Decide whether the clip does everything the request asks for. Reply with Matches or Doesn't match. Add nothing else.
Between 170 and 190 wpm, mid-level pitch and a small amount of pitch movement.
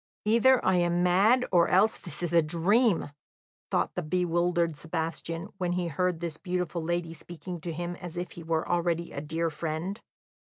Matches